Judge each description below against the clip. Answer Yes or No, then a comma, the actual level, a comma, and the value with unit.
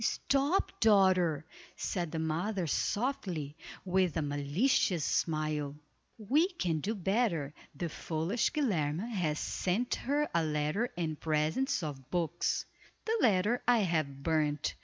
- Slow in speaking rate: Yes, slow, 125 wpm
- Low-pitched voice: No, medium, 175 Hz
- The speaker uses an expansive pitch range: Yes, wide, 6.1 semitones